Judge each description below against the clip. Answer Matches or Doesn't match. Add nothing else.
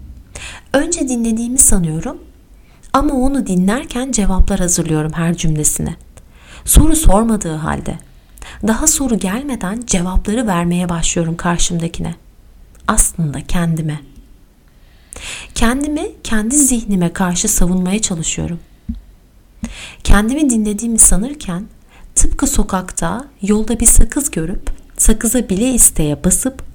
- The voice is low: Doesn't match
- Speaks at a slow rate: Matches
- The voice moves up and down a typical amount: Doesn't match